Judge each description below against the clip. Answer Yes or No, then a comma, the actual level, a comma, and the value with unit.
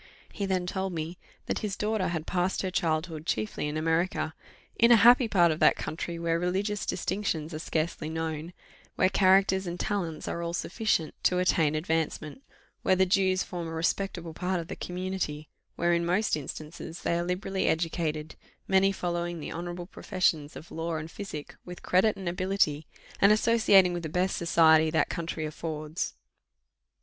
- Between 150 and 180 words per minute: Yes, average, 170 wpm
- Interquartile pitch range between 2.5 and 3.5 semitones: Yes, average, 2.9 semitones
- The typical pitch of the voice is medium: Yes, medium, 175 Hz